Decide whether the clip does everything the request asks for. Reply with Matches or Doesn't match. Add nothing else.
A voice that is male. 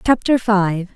Doesn't match